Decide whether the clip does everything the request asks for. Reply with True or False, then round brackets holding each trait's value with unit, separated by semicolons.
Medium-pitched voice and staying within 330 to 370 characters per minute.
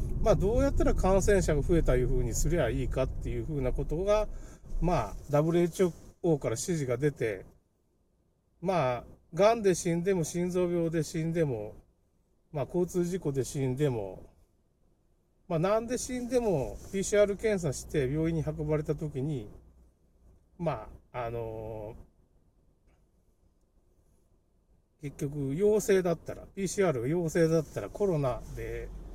False (150 Hz; 245 characters per minute)